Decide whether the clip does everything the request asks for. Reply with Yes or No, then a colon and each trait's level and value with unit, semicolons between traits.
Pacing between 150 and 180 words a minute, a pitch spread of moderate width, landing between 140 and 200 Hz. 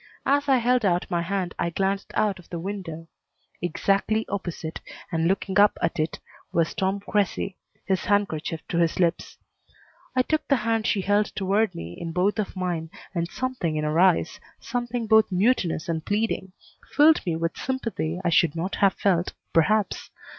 Yes: average, 175 wpm; average, 4.1 semitones; high, 190 Hz